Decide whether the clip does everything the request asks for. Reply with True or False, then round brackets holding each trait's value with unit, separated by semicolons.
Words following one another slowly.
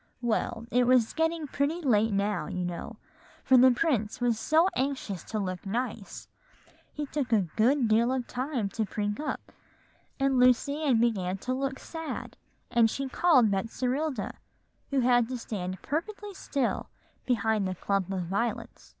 False (160 wpm)